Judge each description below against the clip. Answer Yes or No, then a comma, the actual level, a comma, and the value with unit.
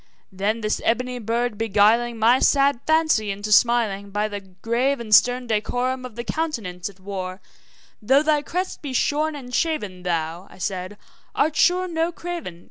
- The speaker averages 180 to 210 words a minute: No, average, 165 wpm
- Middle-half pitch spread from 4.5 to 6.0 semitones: Yes, wide, 5.6 semitones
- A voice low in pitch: No, high, 235 Hz